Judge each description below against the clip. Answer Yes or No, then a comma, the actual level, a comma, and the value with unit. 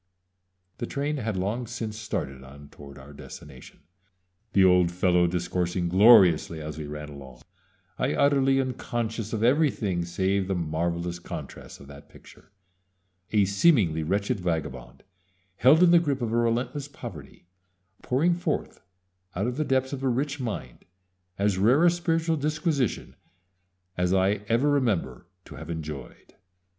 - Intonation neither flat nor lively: No, wide, 7.7 semitones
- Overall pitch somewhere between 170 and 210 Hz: No, low, 100 Hz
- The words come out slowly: No, average, 145 wpm